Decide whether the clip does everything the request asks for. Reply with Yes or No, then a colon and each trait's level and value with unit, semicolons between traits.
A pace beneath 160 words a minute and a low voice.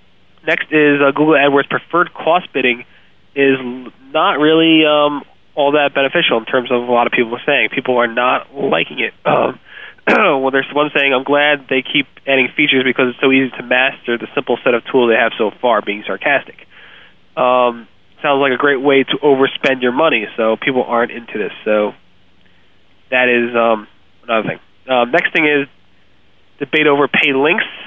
No: average, 185 wpm; low, 130 Hz